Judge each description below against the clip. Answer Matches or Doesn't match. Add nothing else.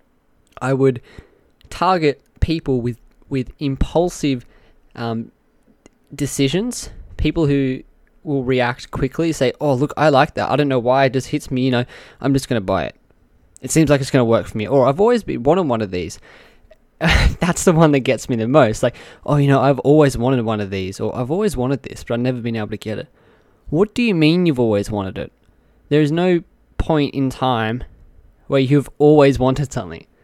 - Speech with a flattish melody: Doesn't match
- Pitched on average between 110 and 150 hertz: Matches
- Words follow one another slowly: Doesn't match